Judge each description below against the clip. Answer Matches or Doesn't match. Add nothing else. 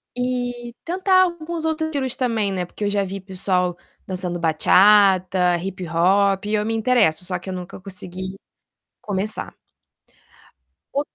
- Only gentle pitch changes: Doesn't match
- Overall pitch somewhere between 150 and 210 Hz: Matches